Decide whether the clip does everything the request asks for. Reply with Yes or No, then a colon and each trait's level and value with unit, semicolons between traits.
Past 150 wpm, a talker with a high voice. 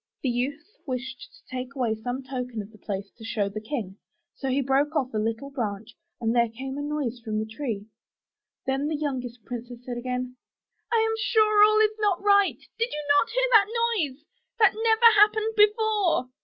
Yes: average, 200 wpm; very high, 265 Hz